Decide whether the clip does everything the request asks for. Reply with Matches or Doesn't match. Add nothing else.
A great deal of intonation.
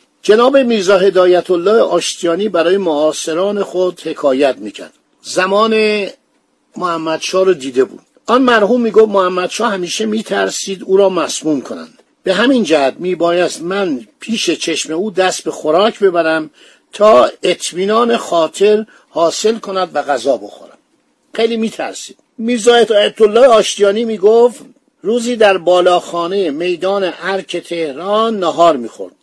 Doesn't match